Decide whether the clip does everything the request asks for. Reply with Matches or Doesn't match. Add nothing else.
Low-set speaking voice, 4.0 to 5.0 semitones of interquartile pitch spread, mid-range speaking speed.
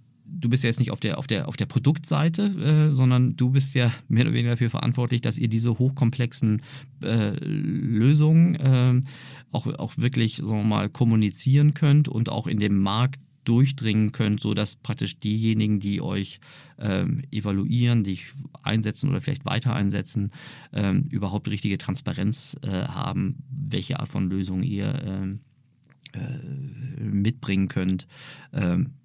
Matches